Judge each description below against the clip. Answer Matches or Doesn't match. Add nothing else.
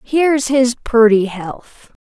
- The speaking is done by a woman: Matches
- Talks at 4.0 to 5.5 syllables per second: Doesn't match